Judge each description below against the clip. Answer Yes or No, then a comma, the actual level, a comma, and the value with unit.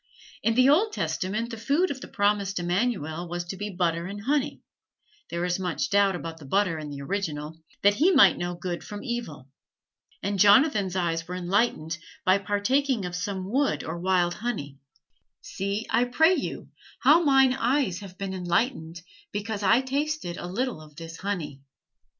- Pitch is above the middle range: Yes, high, 195 Hz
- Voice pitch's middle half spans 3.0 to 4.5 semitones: No, wide, 5.6 semitones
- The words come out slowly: No, average, 175 wpm